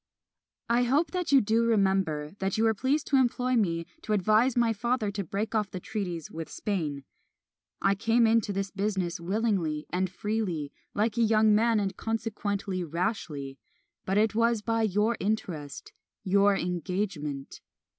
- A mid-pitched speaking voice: No, high, 205 Hz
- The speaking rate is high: No, average, 155 wpm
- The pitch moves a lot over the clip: No, average, 3.8 semitones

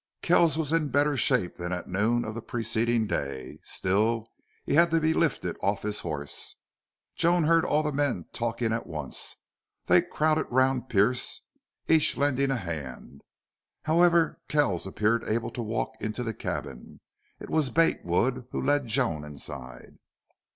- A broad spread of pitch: Yes, wide, 6.7 semitones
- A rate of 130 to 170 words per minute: Yes, average, 160 wpm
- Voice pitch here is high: No, low, 120 Hz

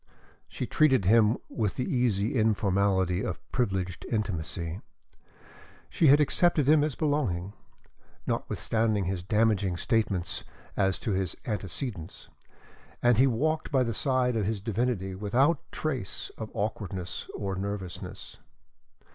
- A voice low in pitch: Yes, low, 105 Hz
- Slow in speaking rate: Yes, slow, 125 wpm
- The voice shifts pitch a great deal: No, average, 4.7 semitones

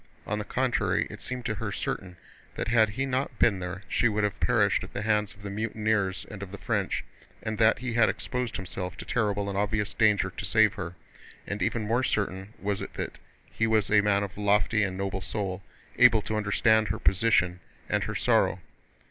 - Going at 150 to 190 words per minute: No, fast, 205 wpm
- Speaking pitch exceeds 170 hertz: No, low, 105 Hz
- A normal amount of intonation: No, narrow, 2.0 semitones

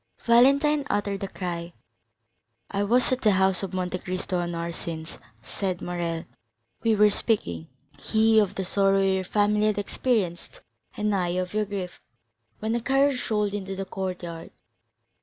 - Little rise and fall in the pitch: No, average, 3.0 semitones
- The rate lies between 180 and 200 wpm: No, average, 160 wpm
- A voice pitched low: No, high, 195 Hz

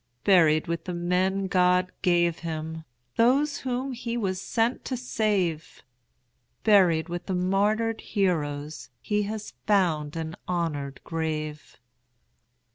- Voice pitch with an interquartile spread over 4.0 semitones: Yes, average, 4.5 semitones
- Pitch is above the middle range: No, medium, 180 Hz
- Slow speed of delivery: Yes, slow, 120 wpm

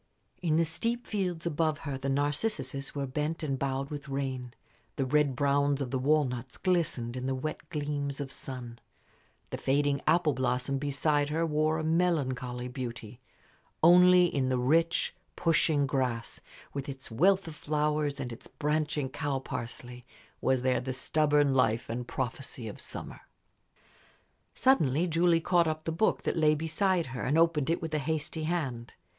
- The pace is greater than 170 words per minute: No, average, 160 wpm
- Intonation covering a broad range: No, average, 3.5 semitones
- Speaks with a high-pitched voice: No, medium, 145 Hz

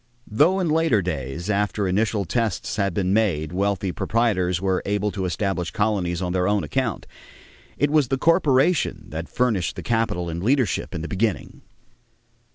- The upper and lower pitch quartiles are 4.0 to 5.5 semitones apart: Yes, average, 4.4 semitones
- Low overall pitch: Yes, low, 100 Hz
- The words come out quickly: No, average, 165 wpm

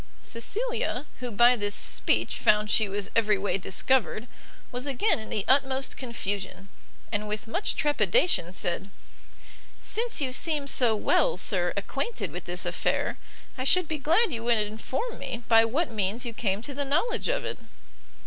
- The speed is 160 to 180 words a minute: Yes, average, 165 wpm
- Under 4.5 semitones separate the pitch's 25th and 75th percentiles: No, wide, 5.6 semitones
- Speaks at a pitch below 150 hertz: No, high, 240 Hz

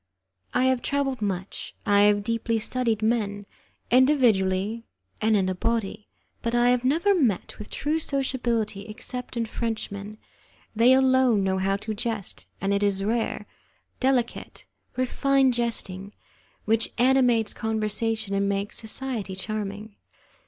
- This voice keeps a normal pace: No, slow, 130 wpm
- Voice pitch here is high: Yes, high, 225 Hz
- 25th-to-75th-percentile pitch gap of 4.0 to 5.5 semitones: No, average, 3.6 semitones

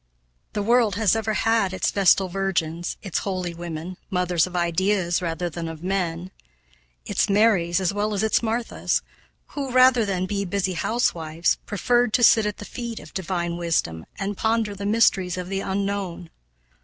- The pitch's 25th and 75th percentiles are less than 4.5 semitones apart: Yes, average, 3.4 semitones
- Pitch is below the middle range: No, high, 195 Hz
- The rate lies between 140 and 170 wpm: Yes, average, 165 wpm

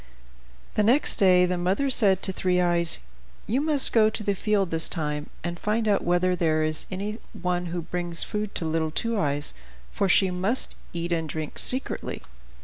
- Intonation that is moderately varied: Yes, average, 3.8 semitones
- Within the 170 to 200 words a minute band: Yes, average, 180 wpm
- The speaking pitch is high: No, medium, 180 Hz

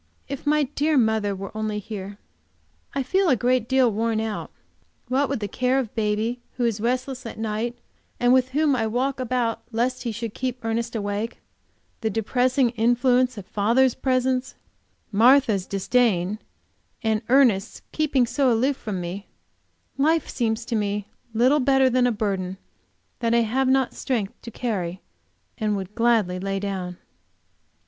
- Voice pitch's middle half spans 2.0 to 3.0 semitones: No, average, 3.4 semitones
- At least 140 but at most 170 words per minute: Yes, average, 155 wpm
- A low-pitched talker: No, high, 235 Hz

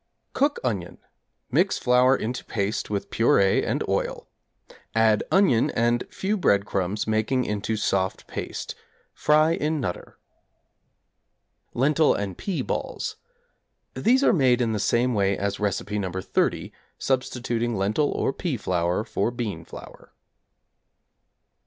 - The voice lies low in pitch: Yes, low, 115 Hz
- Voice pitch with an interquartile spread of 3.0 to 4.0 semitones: No, average, 4.6 semitones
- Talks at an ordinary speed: No, slow, 125 wpm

